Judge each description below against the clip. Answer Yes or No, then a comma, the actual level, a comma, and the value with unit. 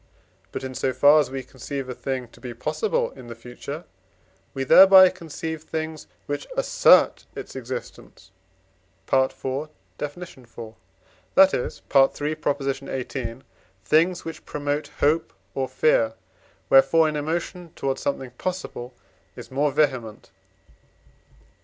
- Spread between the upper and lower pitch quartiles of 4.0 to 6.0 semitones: No, average, 3.5 semitones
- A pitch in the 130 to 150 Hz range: Yes, medium, 140 Hz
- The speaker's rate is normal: No, slow, 125 wpm